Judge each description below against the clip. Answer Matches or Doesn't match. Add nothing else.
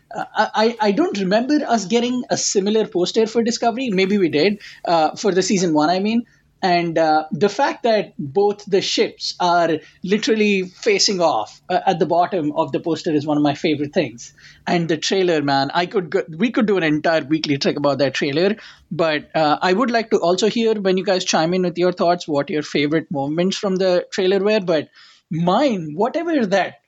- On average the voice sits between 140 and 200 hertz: Matches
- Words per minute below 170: Doesn't match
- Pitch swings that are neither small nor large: Matches